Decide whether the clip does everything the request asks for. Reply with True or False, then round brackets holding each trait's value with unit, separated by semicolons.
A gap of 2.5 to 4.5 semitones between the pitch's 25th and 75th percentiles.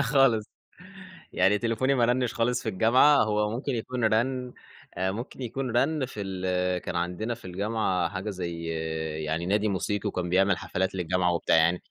False (4.9 semitones)